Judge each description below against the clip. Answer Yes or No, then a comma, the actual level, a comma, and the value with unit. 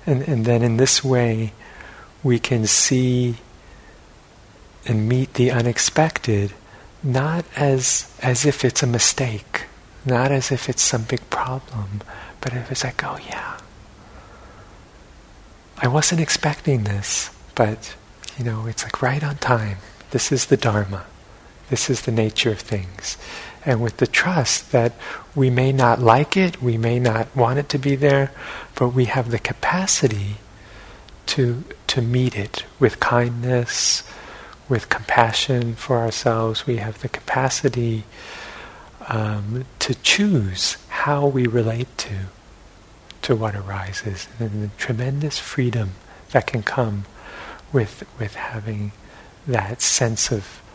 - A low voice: Yes, low, 120 Hz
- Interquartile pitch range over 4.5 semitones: No, average, 3.3 semitones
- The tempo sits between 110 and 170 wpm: Yes, slow, 135 wpm